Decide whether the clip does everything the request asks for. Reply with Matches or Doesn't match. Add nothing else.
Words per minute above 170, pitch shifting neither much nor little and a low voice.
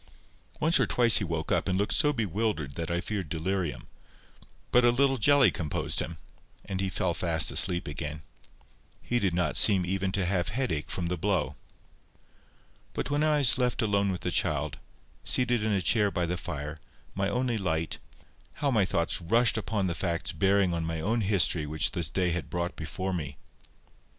Matches